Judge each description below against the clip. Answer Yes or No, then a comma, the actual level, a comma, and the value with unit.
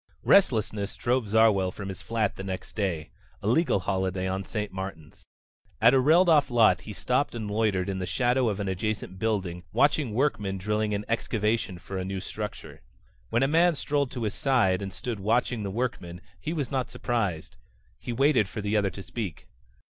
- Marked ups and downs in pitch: No, average, 4.2 semitones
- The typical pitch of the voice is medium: No, low, 105 Hz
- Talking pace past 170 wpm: Yes, average, 190 wpm